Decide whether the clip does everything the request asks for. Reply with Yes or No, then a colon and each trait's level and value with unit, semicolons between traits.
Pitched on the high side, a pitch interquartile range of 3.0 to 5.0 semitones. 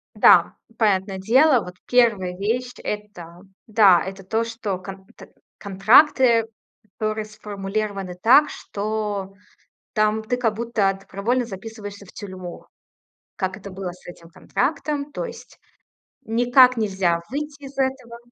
Yes: high, 215 Hz; average, 3.7 semitones